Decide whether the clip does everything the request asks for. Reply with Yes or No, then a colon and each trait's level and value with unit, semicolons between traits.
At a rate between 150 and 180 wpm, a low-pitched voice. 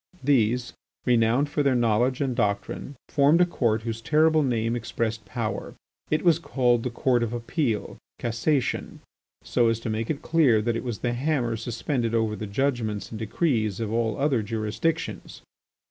Yes: average, 165 wpm; low, 120 Hz